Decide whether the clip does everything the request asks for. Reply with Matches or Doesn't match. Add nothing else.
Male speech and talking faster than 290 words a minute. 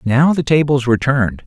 Doesn't match